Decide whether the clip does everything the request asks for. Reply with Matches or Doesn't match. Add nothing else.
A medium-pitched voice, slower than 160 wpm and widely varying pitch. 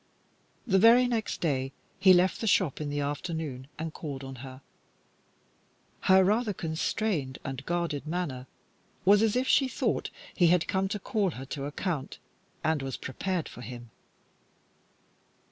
Matches